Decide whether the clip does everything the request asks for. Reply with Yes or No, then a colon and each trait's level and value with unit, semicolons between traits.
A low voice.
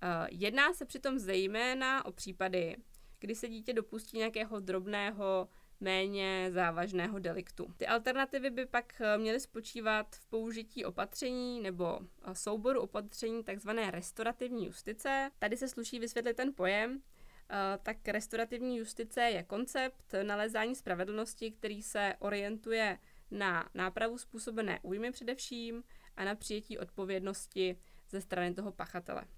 No: high, 220 Hz